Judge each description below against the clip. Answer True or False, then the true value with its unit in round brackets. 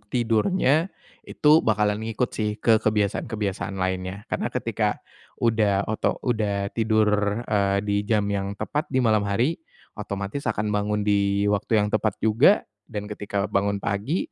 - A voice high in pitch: False (105 Hz)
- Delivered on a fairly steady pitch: True (1.9 semitones)